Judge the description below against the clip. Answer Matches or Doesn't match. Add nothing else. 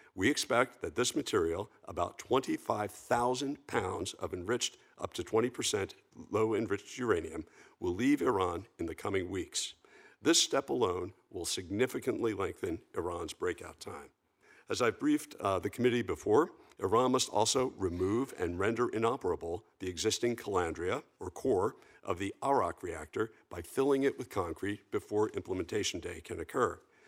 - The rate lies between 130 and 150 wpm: Matches